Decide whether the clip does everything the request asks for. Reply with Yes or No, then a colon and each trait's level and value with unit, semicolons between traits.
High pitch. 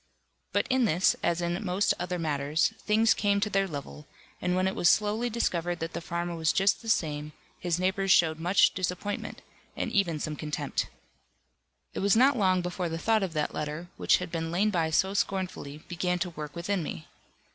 No: medium, 180 Hz